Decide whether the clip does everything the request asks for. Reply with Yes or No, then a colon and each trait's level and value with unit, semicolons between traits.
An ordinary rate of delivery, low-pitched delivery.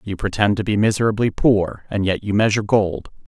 Yes: average, 195 wpm; low, 100 Hz